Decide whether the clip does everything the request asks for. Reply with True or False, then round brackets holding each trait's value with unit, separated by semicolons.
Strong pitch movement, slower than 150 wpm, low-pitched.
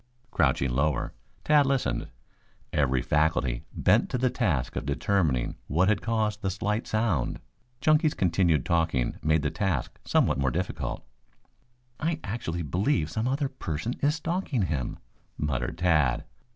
True (8.3 semitones; 140 wpm; 85 Hz)